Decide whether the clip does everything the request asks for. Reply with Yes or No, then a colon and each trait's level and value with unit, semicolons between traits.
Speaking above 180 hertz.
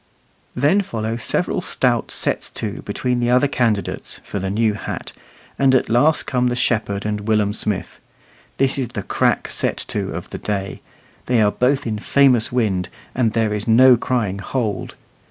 No: low, 115 Hz